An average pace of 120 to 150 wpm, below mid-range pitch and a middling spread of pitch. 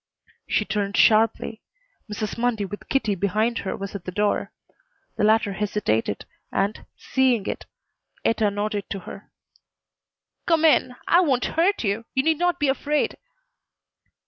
No: average, 145 wpm; high, 215 Hz; average, 4.6 semitones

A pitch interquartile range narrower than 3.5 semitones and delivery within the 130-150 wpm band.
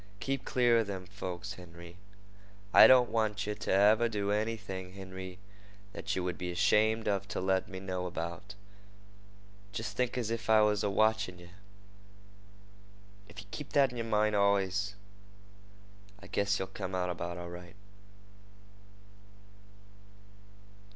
Yes: average, 2.7 semitones; average, 140 wpm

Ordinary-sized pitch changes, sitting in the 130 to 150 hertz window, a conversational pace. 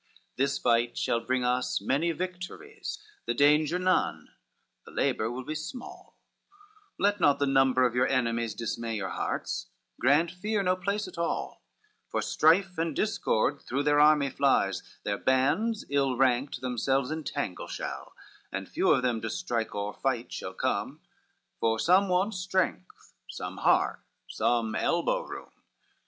No: wide, 6.7 semitones; medium, 140 Hz; average, 150 wpm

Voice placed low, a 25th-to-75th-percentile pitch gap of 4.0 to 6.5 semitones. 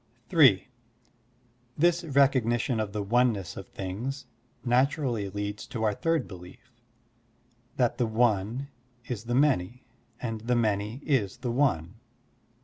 Yes: low, 120 Hz; average, 4.4 semitones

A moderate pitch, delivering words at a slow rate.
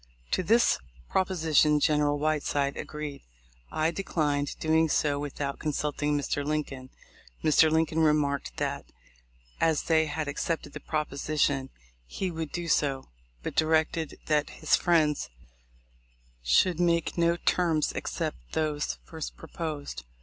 Yes: medium, 150 Hz; slow, 120 wpm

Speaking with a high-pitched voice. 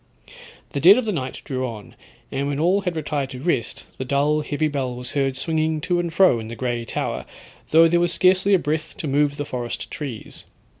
No: medium, 145 Hz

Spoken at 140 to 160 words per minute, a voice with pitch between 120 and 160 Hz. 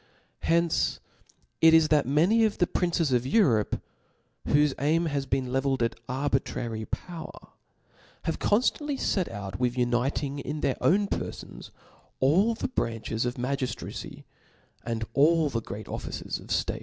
Yes: average, 145 wpm; medium, 140 Hz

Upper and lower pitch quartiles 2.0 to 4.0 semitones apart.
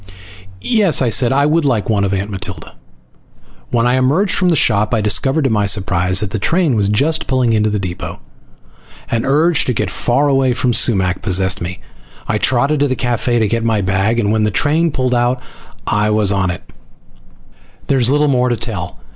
No: average, 4.8 semitones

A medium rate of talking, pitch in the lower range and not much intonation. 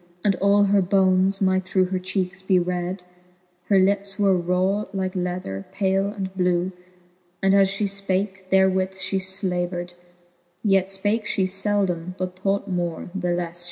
No: average, 160 wpm; high, 190 Hz; narrow, 1.3 semitones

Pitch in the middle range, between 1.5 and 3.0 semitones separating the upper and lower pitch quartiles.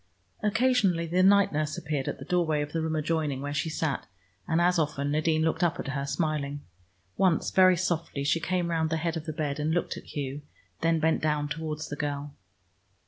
Yes: medium, 160 Hz; narrow, 2.4 semitones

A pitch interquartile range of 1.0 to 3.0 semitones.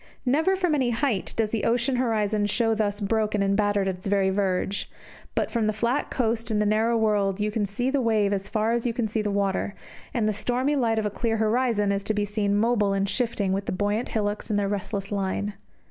Yes: narrow, 2.4 semitones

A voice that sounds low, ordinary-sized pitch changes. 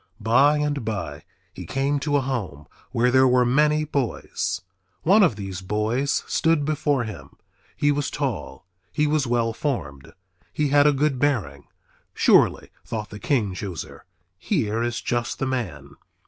No: low, 125 Hz; wide, 5.8 semitones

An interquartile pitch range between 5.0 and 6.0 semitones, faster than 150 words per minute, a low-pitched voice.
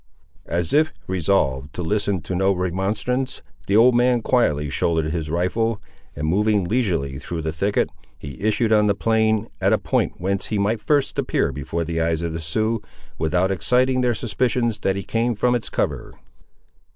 Yes: wide, 5.4 semitones; average, 175 wpm; low, 100 Hz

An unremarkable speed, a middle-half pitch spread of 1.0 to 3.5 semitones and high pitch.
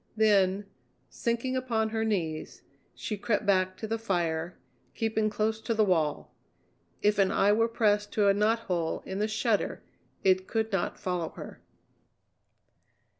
Yes: average, 145 wpm; average, 2.9 semitones; high, 210 Hz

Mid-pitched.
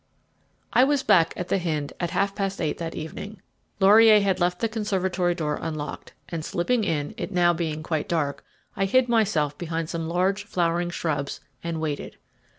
Yes: medium, 175 Hz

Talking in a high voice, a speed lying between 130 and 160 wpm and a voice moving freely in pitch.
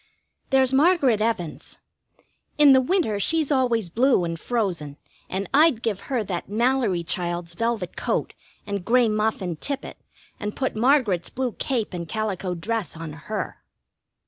Yes: high, 220 Hz; average, 145 wpm; wide, 6.3 semitones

